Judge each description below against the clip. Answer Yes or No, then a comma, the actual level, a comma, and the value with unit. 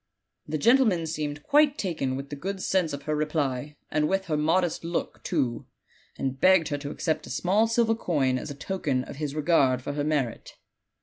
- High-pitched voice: No, medium, 155 Hz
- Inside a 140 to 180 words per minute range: No, average, 200 wpm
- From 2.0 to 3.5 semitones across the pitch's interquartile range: No, average, 4.5 semitones